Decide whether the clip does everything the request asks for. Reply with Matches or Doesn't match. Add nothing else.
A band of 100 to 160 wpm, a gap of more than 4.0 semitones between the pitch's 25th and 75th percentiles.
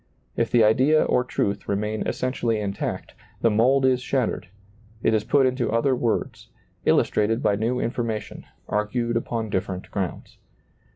Doesn't match